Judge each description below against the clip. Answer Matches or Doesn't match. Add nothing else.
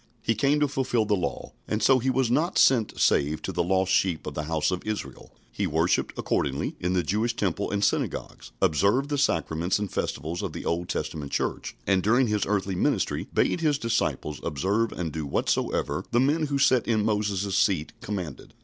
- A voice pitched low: Matches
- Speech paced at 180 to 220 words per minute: Matches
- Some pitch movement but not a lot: Doesn't match